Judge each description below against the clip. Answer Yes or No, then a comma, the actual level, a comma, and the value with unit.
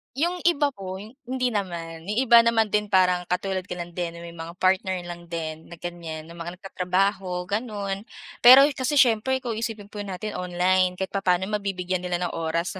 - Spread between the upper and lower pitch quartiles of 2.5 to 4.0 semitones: Yes, average, 3.3 semitones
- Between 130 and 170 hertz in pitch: No, medium, 185 Hz